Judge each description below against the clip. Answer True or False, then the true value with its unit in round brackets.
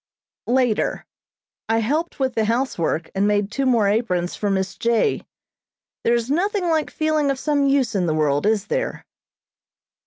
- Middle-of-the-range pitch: False (235 Hz)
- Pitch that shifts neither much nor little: False (5.7 semitones)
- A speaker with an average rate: True (160 wpm)